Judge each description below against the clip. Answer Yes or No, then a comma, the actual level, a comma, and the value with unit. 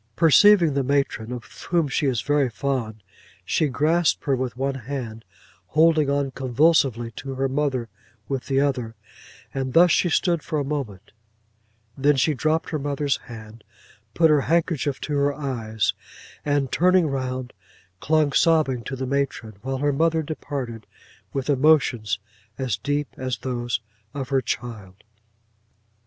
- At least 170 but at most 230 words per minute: No, average, 145 wpm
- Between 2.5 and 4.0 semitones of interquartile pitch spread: Yes, average, 3.2 semitones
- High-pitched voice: No, low, 135 Hz